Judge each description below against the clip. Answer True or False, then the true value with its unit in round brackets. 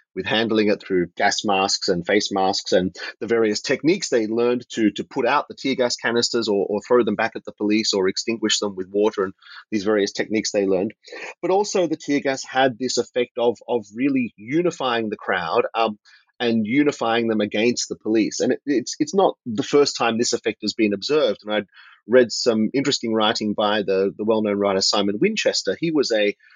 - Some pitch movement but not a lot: True (3.1 semitones)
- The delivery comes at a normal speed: False (210 wpm)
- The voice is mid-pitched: False (110 Hz)